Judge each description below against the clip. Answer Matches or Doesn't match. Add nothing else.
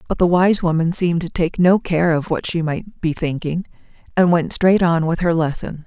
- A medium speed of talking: Doesn't match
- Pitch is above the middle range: Doesn't match